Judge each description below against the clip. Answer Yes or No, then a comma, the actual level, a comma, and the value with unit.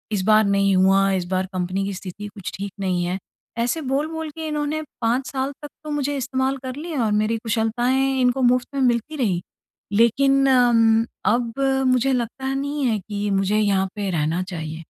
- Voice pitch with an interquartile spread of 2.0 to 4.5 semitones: No, wide, 5.4 semitones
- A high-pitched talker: Yes, high, 235 Hz